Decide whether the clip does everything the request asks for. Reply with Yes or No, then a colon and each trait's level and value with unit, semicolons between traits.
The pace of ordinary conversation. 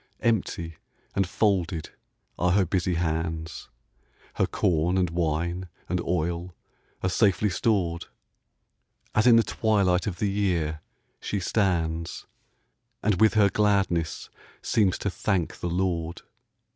No: slow, 120 wpm